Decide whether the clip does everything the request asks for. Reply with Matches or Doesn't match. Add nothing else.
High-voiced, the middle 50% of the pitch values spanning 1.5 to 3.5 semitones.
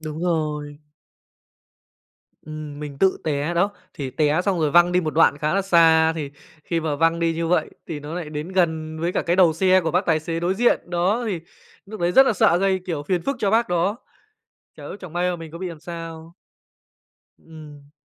Doesn't match